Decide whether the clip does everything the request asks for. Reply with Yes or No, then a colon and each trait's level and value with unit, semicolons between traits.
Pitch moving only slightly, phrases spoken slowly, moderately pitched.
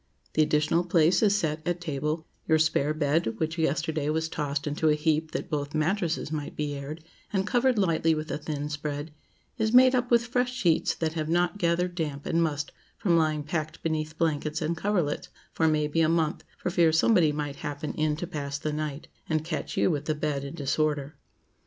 No: narrow, 2.2 semitones; average, 200 wpm; medium, 155 Hz